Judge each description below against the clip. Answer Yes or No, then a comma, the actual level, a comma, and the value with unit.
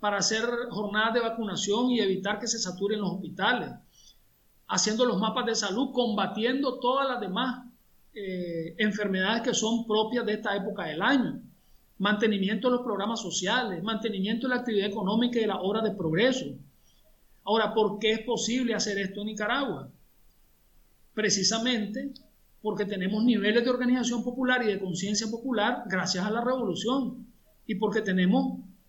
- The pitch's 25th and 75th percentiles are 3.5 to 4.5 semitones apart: No, average, 3.0 semitones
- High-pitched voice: Yes, high, 220 Hz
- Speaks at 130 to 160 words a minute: Yes, average, 155 wpm